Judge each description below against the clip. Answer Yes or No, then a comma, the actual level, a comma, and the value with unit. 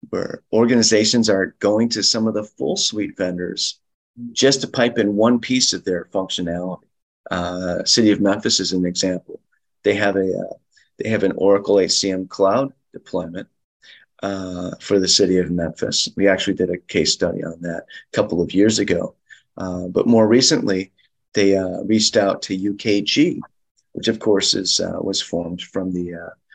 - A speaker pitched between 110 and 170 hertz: No, low, 100 Hz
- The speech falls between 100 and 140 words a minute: No, average, 175 wpm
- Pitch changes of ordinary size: Yes, average, 3.5 semitones